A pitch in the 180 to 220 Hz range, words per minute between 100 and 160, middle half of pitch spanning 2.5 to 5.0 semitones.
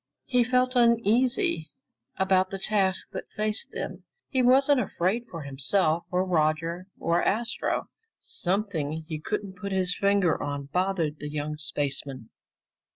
No: medium, 185 Hz; slow, 135 wpm; wide, 5.4 semitones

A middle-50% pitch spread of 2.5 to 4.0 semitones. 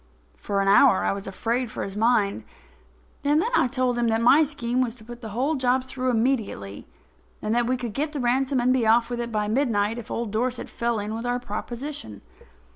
Yes: average, 2.8 semitones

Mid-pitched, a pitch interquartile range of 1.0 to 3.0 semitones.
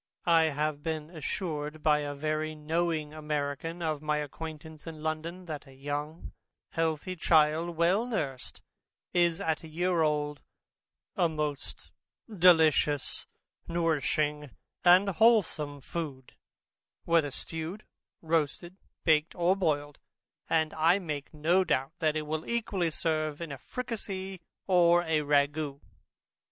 Yes: medium, 155 Hz; narrow, 2.4 semitones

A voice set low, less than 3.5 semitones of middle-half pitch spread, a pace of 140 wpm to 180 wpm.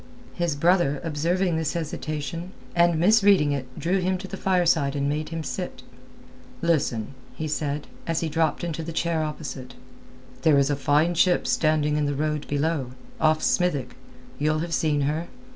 No: medium, 155 Hz; average, 2.8 semitones; average, 165 wpm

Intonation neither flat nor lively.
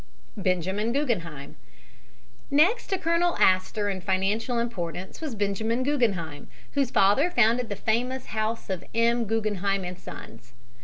Yes: average, 4.8 semitones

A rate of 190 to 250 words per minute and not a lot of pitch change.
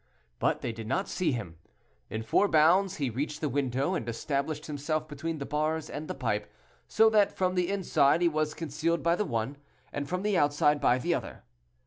No: average, 200 wpm; average, 3.6 semitones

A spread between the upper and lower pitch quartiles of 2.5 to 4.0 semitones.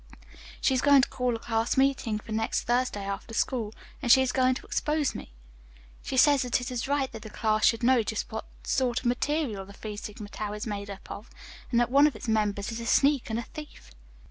Yes: average, 3.4 semitones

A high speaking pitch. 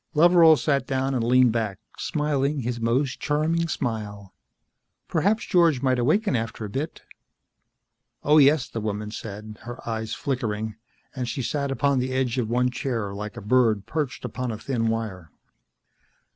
No: low, 125 Hz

